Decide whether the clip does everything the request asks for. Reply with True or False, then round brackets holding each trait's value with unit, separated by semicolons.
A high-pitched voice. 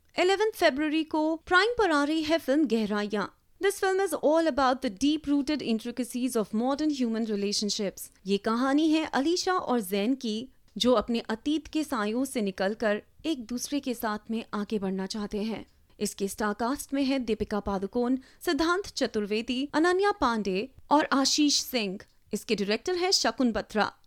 True (250 Hz)